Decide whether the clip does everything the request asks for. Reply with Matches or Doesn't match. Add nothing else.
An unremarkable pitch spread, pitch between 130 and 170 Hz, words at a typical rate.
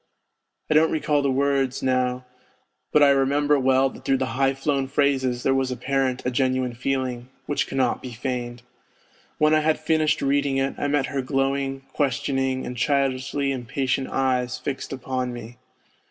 Doesn't match